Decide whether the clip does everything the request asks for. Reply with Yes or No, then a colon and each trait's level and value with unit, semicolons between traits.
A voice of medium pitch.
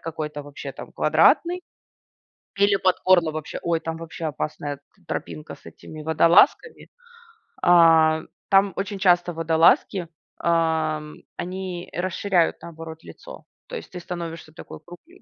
Yes: medium, 165 Hz